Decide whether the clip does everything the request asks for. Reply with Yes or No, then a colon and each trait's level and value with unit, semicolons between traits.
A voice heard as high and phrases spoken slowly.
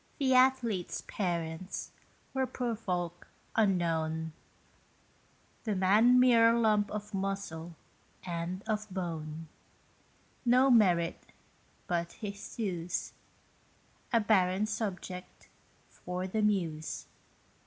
Yes: high, 195 Hz; slow, 90 wpm